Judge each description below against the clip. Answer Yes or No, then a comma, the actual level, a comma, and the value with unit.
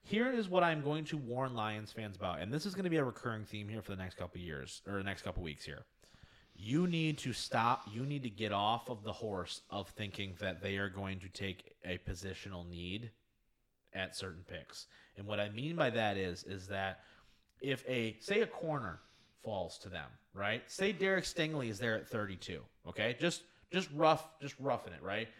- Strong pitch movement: Yes, wide, 6.5 semitones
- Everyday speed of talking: No, fast, 215 wpm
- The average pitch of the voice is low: Yes, low, 110 Hz